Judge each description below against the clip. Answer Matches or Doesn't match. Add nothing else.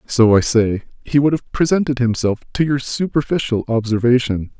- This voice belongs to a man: Matches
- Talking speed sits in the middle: Matches